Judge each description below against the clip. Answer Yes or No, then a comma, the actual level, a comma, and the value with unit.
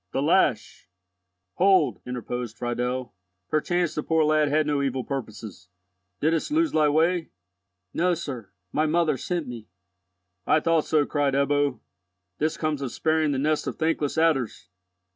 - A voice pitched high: No, medium, 150 Hz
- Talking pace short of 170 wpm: Yes, average, 145 wpm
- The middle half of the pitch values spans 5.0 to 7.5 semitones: No, average, 3.7 semitones